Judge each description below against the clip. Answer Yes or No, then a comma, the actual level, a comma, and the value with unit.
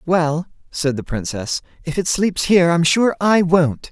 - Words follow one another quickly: No, average, 185 wpm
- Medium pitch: Yes, medium, 165 Hz